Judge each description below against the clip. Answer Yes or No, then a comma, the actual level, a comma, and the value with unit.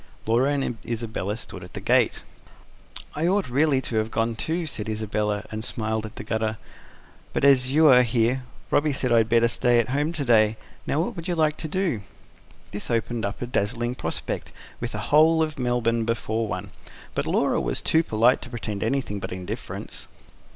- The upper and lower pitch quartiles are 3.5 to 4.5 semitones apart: Yes, average, 4.2 semitones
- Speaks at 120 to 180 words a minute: No, average, 195 wpm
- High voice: No, low, 120 Hz